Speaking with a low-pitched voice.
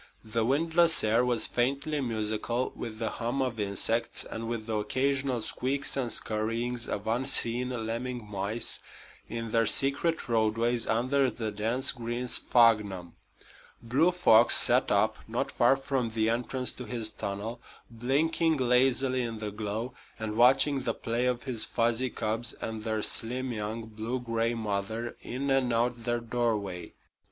Yes: low, 120 Hz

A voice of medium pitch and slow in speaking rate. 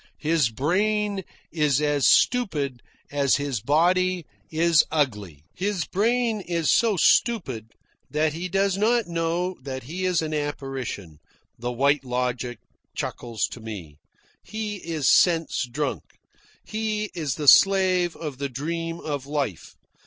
Yes: medium, 155 Hz; slow, 130 wpm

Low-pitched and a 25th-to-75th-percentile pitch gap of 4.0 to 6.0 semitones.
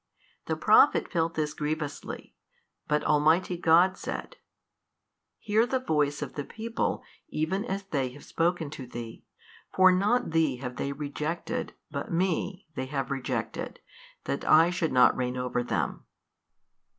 No: medium, 155 Hz; average, 4.8 semitones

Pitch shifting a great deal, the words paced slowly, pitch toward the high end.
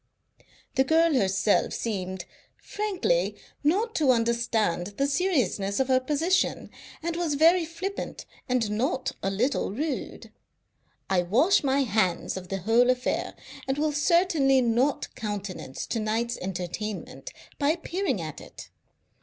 Yes: wide, 7.3 semitones; slow, 130 wpm; very high, 255 Hz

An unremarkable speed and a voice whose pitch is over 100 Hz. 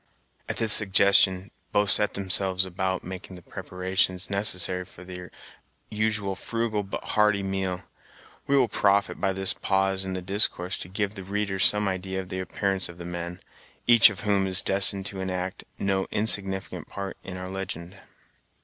No: average, 165 wpm; very low, 95 Hz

